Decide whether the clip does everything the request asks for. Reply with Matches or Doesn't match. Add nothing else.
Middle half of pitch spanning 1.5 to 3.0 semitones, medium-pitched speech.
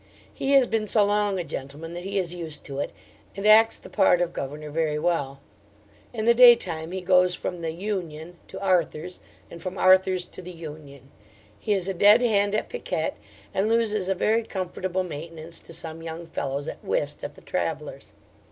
Doesn't match